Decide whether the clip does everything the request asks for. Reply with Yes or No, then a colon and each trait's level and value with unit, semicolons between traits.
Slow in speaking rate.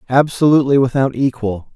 Yes: slow, 100 wpm